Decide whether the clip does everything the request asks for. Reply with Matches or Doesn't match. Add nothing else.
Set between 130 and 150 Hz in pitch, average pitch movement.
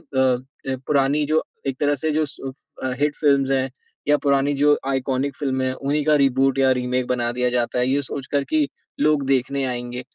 Doesn't match